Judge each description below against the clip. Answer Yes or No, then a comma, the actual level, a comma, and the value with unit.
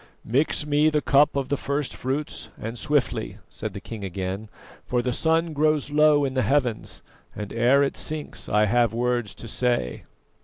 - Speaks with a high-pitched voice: No, low, 130 Hz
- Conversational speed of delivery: Yes, average, 180 wpm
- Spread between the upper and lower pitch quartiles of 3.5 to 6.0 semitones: Yes, average, 4.2 semitones